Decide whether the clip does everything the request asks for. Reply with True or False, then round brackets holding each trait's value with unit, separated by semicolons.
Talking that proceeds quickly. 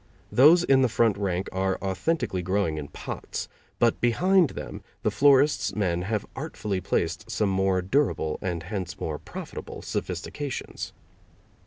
False (140 wpm)